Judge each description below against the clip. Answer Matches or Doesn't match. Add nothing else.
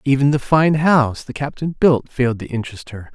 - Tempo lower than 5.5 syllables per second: Doesn't match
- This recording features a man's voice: Matches